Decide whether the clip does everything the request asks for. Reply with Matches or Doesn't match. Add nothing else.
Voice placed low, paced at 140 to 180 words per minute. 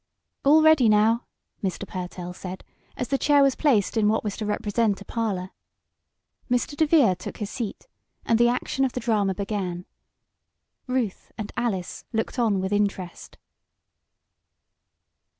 Doesn't match